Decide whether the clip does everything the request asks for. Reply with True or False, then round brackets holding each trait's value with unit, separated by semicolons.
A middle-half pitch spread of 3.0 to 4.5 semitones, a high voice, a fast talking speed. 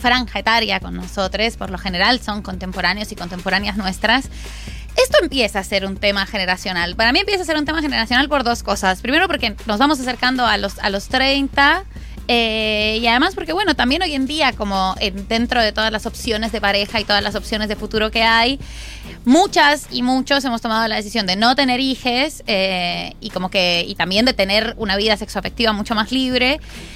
True (4.2 semitones; 225 Hz; 200 wpm)